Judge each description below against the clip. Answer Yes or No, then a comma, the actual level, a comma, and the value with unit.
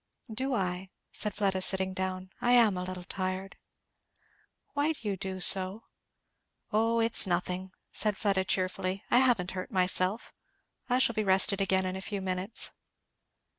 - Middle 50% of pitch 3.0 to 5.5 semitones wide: No, narrow, 2.6 semitones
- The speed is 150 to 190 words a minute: Yes, average, 155 wpm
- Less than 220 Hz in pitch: Yes, high, 190 Hz